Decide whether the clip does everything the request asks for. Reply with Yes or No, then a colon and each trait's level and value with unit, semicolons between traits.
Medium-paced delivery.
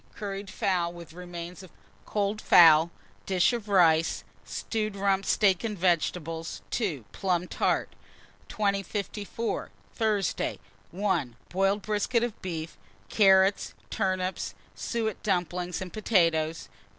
No: slow, 110 wpm